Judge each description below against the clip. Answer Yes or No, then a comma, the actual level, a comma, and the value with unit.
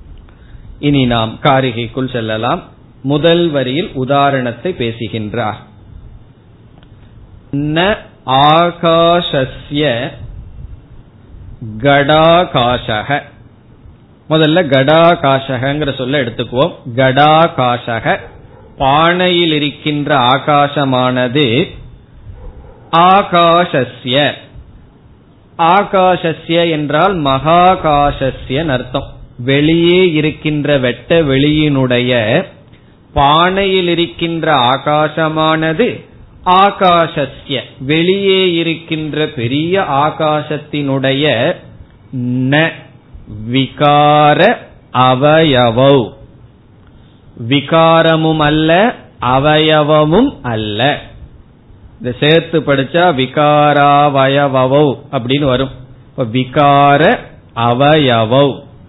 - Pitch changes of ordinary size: Yes, average, 4.2 semitones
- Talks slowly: Yes, slow, 45 wpm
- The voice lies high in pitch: No, medium, 140 Hz